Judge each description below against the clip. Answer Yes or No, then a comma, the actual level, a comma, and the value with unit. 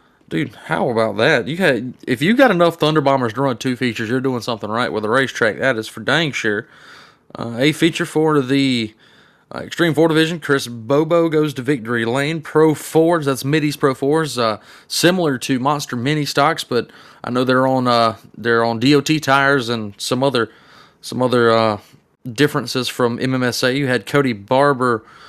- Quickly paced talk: No, average, 185 wpm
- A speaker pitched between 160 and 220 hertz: No, low, 135 Hz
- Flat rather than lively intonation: No, average, 3.9 semitones